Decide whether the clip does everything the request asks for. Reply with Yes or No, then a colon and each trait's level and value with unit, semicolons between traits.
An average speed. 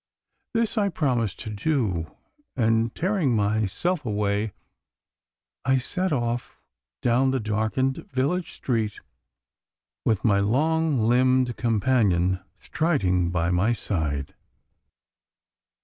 No: slow, 100 wpm